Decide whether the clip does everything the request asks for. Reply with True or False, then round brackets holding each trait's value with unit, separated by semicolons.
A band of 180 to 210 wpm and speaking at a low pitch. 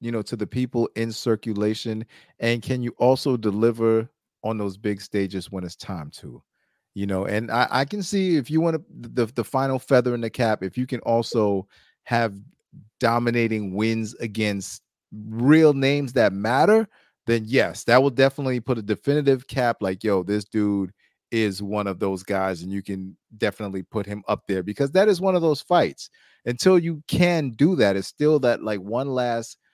True (190 wpm; 115 Hz)